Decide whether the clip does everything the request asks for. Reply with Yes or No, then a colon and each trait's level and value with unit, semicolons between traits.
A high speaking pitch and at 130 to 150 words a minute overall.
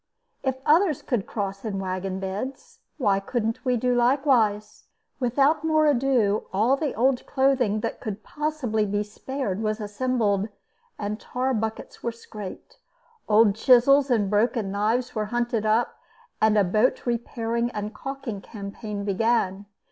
Yes: high, 225 Hz; average, 140 wpm